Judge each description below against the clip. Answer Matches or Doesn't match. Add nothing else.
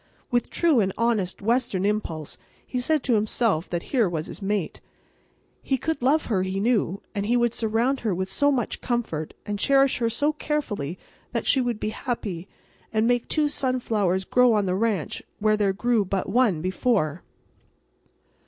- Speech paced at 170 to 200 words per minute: Matches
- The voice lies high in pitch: Matches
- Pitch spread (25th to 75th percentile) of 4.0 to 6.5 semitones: Matches